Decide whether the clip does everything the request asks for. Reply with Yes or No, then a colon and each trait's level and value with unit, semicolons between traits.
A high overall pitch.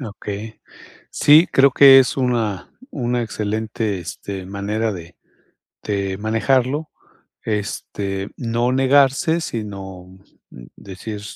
No: low, 110 Hz